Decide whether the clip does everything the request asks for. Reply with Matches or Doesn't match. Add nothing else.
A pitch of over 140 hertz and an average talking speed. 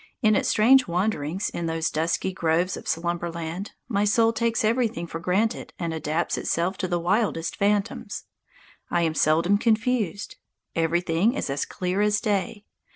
Matches